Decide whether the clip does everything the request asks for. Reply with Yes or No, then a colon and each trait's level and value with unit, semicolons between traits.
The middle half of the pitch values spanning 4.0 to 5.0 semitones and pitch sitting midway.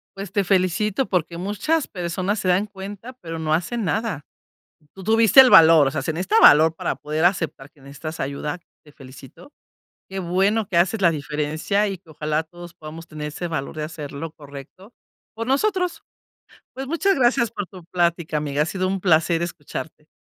Yes: average, 4.7 semitones; medium, 175 Hz